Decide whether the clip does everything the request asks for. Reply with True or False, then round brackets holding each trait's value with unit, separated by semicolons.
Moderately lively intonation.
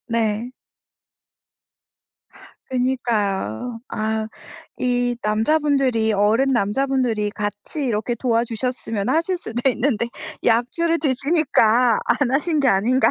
True (3.7 semitones)